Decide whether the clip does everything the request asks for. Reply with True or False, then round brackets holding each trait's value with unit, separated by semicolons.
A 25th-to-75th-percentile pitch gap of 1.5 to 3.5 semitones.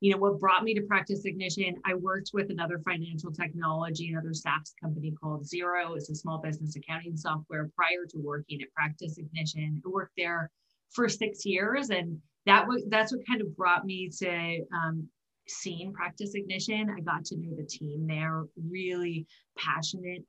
True (3.2 semitones)